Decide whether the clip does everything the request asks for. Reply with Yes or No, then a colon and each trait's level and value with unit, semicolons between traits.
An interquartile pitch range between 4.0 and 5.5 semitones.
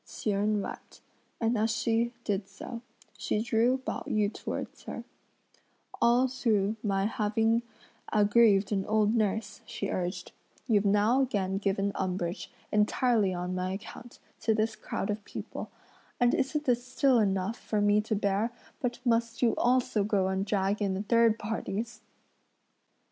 No: average, 2.7 semitones